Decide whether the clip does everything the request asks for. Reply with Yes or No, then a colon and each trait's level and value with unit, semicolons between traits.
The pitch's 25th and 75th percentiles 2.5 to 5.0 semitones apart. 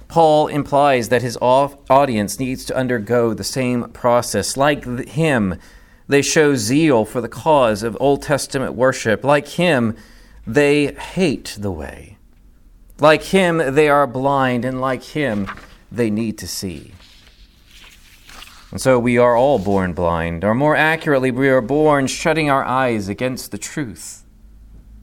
No: wide, 5.4 semitones